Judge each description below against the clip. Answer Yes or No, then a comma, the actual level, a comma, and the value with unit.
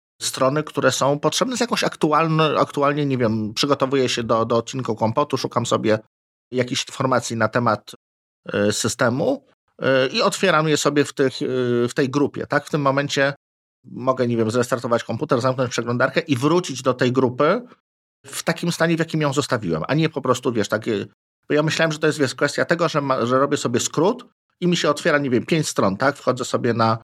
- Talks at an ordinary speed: No, fast, 205 wpm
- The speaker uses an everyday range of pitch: Yes, average, 3.7 semitones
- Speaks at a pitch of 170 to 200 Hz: No, low, 135 Hz